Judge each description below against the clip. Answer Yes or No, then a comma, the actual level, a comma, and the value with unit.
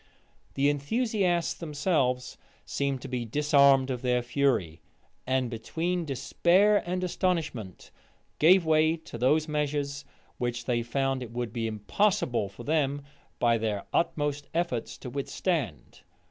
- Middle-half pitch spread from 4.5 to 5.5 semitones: Yes, average, 4.8 semitones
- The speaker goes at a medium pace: No, slow, 130 wpm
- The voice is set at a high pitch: No, medium, 140 Hz